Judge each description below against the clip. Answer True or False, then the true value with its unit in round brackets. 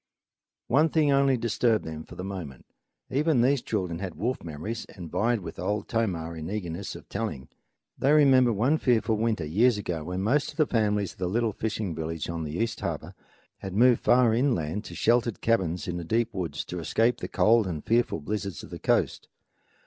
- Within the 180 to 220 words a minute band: True (200 wpm)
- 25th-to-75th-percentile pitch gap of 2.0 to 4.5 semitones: False (5.5 semitones)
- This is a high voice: False (105 Hz)